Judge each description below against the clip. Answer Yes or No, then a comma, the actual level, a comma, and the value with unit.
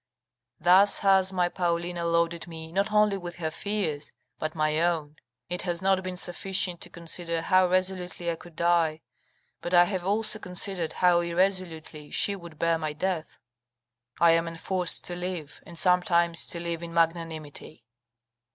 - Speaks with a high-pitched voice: No, medium, 175 Hz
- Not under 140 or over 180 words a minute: Yes, average, 160 wpm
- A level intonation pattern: Yes, narrow, 1.9 semitones